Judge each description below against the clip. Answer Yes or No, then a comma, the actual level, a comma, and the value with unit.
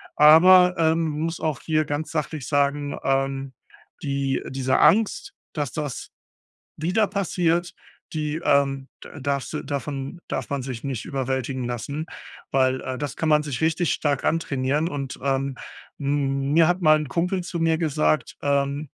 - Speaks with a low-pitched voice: No, medium, 145 Hz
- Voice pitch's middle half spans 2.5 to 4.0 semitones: Yes, average, 2.9 semitones